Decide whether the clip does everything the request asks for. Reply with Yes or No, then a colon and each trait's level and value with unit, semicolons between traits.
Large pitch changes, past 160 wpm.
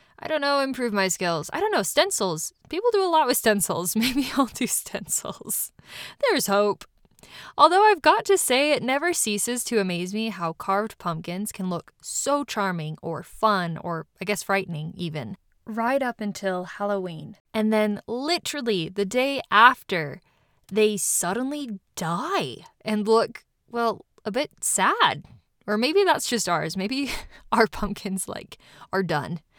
No: wide, 5.9 semitones; average, 155 wpm